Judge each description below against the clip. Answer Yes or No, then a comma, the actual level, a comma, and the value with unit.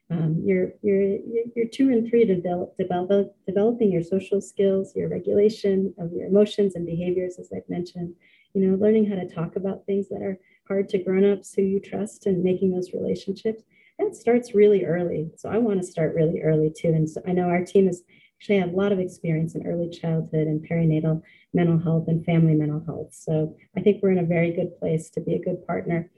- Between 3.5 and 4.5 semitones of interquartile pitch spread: No, average, 3.1 semitones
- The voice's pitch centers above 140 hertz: Yes, medium, 185 Hz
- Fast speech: Yes, fast, 215 wpm